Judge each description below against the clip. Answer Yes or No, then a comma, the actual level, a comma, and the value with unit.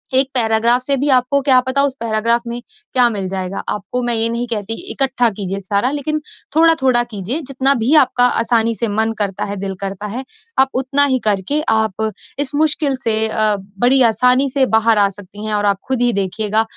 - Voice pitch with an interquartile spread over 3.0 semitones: Yes, average, 3.8 semitones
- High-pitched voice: Yes, high, 235 Hz